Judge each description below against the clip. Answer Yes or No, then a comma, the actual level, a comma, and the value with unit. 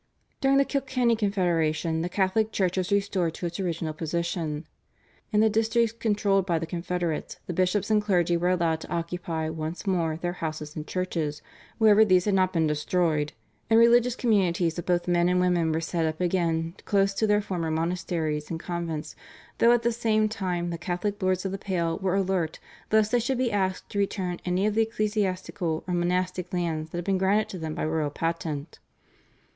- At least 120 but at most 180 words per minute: No, average, 195 wpm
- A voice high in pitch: No, medium, 180 Hz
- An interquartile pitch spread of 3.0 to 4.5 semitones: Yes, average, 3.6 semitones